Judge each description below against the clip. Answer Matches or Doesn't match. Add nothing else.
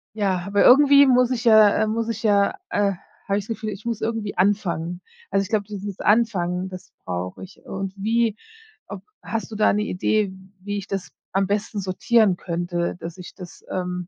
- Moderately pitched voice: Doesn't match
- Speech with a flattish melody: Doesn't match